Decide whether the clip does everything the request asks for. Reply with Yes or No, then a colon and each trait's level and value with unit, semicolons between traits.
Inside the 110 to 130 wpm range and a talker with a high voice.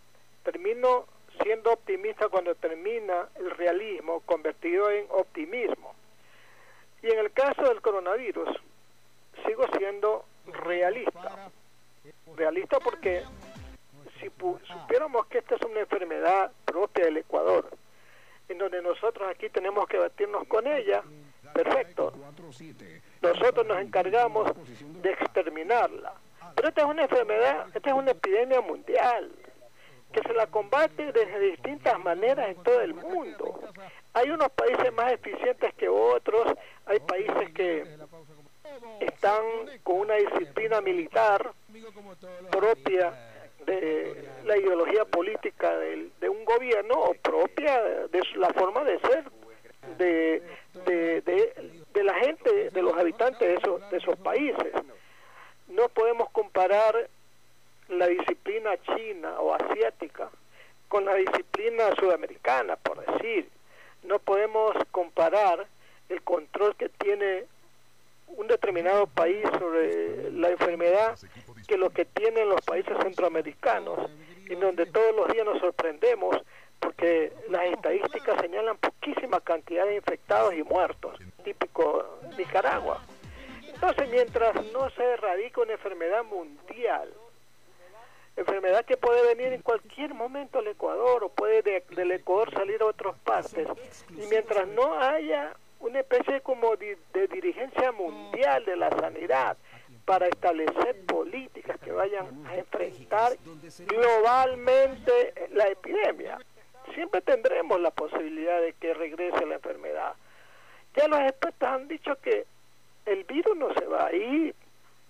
Yes: slow, 125 wpm; very high, 255 Hz